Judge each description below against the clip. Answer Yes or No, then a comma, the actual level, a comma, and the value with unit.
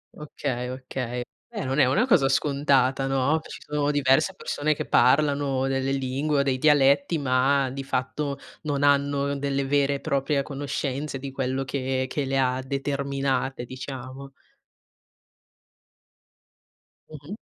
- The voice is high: No, low, 135 Hz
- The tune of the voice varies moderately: No, narrow, 1.4 semitones